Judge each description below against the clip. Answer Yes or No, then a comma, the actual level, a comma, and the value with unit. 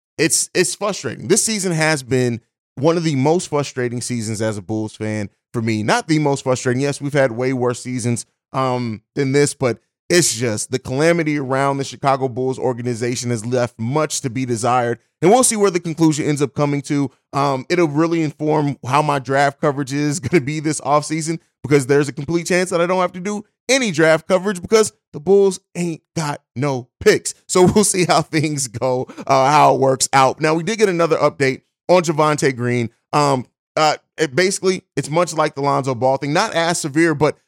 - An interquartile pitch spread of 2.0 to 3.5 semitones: No, average, 4.4 semitones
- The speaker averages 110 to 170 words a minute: No, fast, 205 wpm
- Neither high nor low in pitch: Yes, medium, 145 Hz